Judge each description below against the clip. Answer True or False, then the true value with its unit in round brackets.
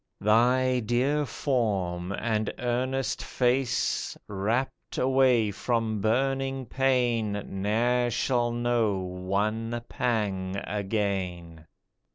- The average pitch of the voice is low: True (115 Hz)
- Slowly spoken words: True (85 wpm)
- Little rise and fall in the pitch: False (3.7 semitones)